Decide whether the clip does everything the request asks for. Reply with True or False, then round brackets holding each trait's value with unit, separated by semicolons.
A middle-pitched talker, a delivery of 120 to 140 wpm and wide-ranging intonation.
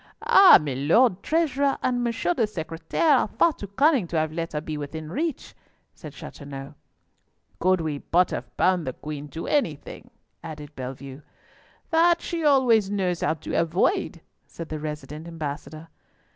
False (165 Hz; 155 wpm; 8.7 semitones)